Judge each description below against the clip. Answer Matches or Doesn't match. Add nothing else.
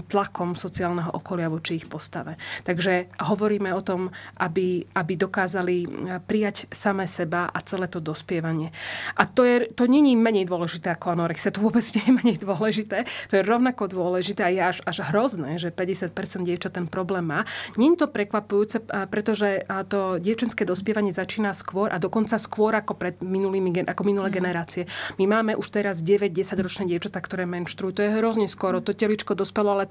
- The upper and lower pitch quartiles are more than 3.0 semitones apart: Doesn't match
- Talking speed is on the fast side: Matches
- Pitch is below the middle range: Doesn't match